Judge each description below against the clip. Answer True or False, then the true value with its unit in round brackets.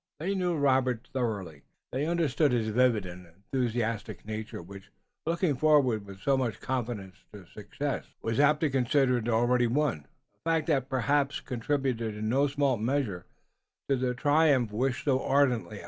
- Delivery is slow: False (160 wpm)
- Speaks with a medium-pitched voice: False (125 Hz)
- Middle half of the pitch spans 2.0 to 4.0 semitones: False (4.5 semitones)